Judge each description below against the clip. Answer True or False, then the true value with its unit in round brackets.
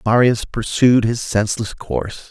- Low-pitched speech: True (115 Hz)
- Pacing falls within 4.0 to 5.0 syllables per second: True (4.6 syllables/s)